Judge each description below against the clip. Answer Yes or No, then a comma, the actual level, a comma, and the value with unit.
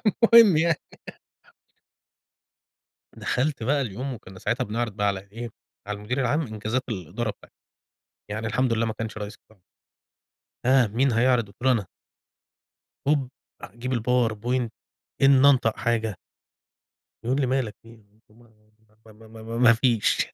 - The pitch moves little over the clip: No, average, 3.1 semitones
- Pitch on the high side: No, low, 115 Hz